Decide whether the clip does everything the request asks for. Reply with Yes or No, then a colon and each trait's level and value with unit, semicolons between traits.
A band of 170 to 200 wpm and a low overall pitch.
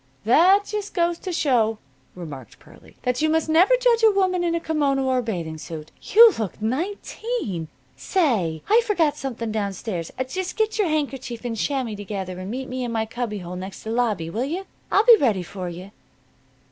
No: average, 190 wpm; very high, 250 Hz